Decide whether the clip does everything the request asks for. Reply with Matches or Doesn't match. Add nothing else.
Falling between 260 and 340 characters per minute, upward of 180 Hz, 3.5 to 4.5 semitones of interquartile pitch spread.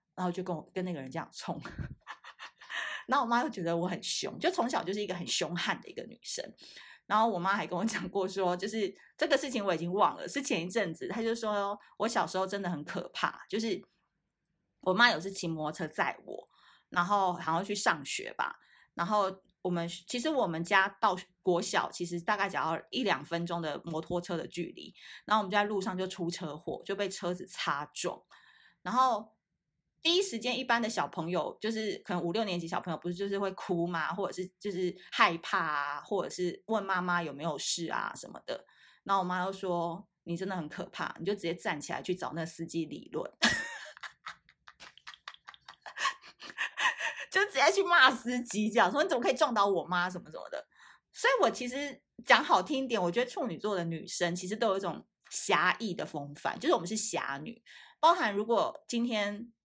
Matches